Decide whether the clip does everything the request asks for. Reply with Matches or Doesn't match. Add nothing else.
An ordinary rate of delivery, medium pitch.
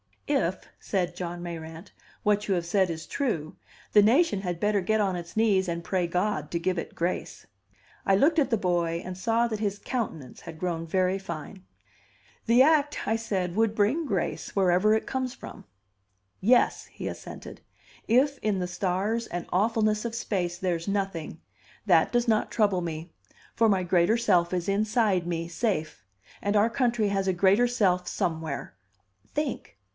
Doesn't match